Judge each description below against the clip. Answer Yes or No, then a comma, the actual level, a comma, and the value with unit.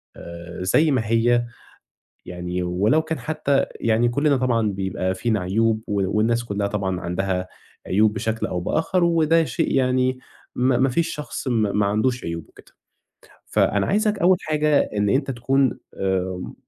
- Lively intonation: Yes, wide, 6.0 semitones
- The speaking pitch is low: Yes, low, 115 Hz